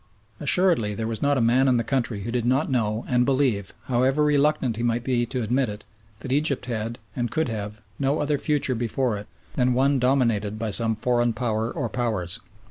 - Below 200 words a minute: No, fast, 205 wpm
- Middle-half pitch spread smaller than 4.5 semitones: Yes, average, 3.2 semitones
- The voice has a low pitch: Yes, low, 120 Hz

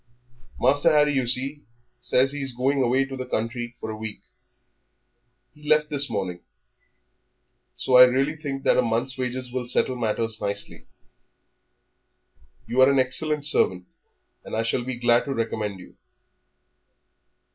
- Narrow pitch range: No, average, 3.0 semitones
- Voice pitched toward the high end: No, low, 125 Hz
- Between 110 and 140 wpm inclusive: No, average, 155 wpm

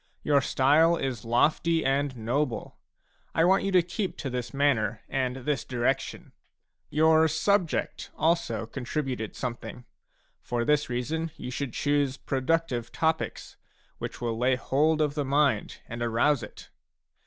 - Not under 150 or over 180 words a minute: No, average, 140 wpm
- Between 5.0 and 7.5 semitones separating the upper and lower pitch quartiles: No, average, 4.3 semitones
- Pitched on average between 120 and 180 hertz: Yes, medium, 140 Hz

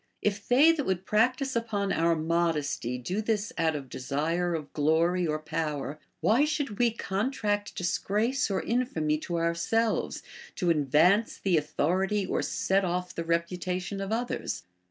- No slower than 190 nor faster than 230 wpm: No, average, 155 wpm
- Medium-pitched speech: Yes, medium, 180 Hz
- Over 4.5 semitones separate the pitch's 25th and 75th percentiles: Yes, average, 4.9 semitones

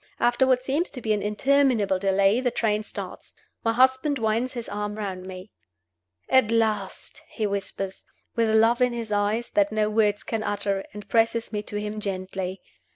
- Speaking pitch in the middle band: No, high, 215 Hz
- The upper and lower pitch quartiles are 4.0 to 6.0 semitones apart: No, average, 2.7 semitones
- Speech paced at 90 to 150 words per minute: No, average, 175 wpm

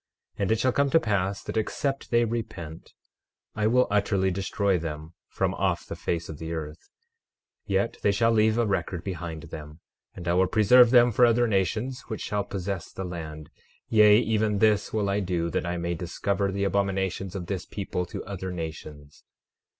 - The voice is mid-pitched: No, low, 100 Hz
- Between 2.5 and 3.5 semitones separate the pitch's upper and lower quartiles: No, average, 3.9 semitones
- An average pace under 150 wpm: No, average, 190 wpm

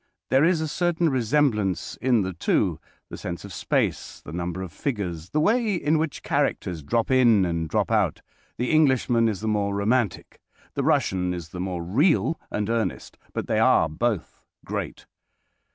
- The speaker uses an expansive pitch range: Yes, wide, 7.5 semitones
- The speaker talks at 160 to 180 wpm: Yes, average, 170 wpm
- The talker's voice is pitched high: No, low, 110 Hz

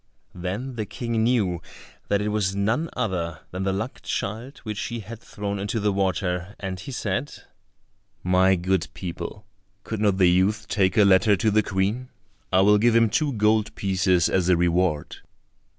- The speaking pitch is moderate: No, low, 100 Hz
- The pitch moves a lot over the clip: No, average, 2.9 semitones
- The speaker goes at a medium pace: Yes, average, 175 wpm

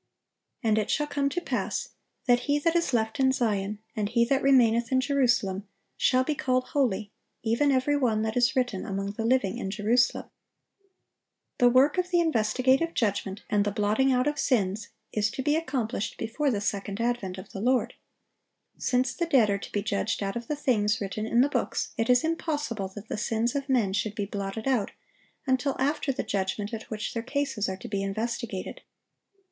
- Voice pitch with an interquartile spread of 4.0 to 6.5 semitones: Yes, average, 4.4 semitones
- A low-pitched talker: No, high, 235 Hz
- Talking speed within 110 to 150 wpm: No, average, 195 wpm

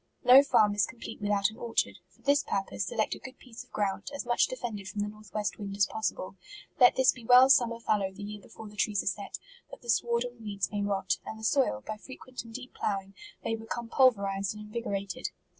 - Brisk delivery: Yes, fast, 230 wpm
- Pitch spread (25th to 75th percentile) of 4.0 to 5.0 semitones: No, average, 3.0 semitones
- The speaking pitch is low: No, high, 215 Hz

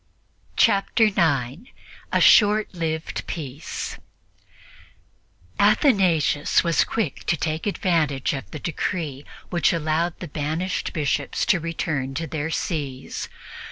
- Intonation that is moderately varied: Yes, average, 3.5 semitones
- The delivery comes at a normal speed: No, slow, 110 wpm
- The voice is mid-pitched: Yes, medium, 160 Hz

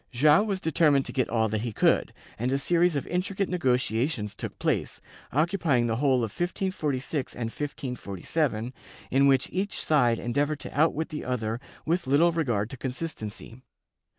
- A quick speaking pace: No, average, 165 wpm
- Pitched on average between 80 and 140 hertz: Yes, low, 135 Hz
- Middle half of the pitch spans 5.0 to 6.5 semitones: Yes, average, 5.3 semitones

